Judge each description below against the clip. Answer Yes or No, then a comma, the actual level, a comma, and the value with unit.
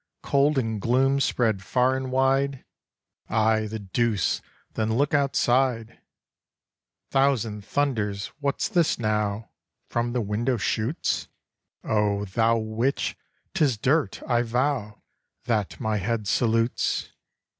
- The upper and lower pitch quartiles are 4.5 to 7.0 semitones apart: No, average, 3.6 semitones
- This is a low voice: Yes, low, 115 Hz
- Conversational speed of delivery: No, slow, 115 wpm